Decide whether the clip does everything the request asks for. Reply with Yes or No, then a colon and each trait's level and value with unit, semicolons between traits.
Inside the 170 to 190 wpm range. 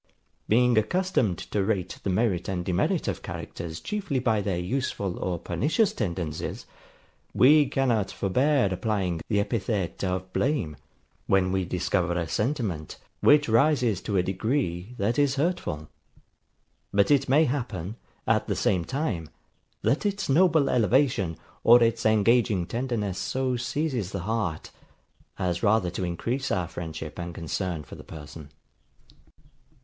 No: average, 140 wpm